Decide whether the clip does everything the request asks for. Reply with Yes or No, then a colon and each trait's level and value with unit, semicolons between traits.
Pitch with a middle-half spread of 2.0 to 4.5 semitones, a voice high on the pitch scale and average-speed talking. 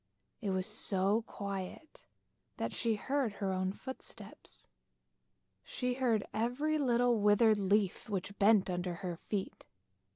No: average, 3.8 semitones; high, 210 Hz; slow, 125 wpm